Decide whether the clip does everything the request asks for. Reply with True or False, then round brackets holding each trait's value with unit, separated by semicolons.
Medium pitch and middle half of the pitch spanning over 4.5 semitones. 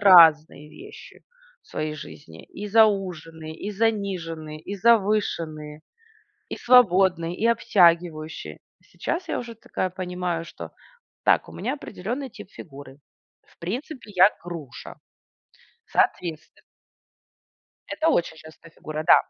True (180 Hz; 4.9 semitones)